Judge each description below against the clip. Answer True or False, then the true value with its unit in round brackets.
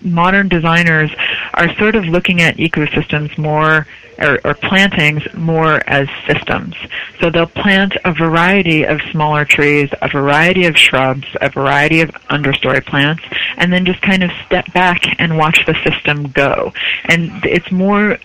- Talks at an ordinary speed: True (155 wpm)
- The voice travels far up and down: False (3.4 semitones)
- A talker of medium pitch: True (165 Hz)